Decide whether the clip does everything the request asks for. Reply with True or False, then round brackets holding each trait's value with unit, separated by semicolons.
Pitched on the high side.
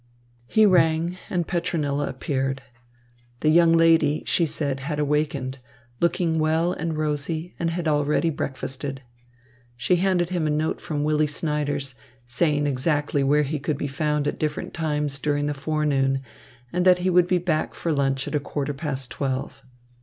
False (150 Hz)